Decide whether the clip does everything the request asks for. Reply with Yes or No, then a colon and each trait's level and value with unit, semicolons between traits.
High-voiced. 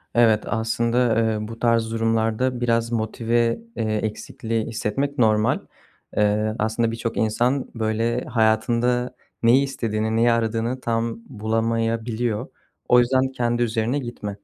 No: low, 115 Hz